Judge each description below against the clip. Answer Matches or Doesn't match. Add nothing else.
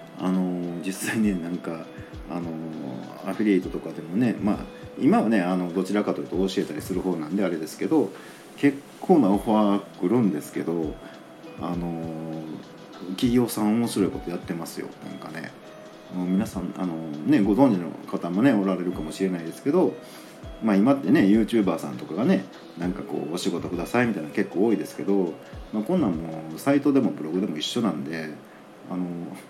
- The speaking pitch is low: Matches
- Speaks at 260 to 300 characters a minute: Doesn't match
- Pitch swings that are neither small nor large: Matches